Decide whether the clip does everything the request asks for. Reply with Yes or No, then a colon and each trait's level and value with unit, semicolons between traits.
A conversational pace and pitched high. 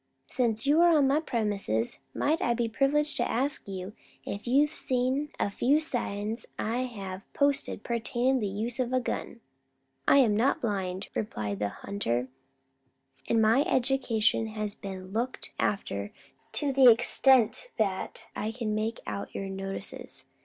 Yes: average, 160 wpm; high, 230 Hz